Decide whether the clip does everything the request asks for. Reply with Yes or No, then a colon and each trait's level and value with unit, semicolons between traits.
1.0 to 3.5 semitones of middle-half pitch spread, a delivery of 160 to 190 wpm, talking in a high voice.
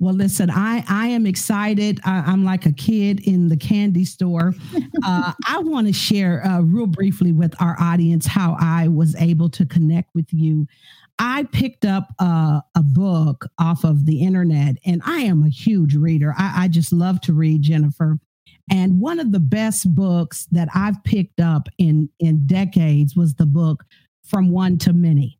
No: average, 3.2 semitones; average, 180 wpm; medium, 175 Hz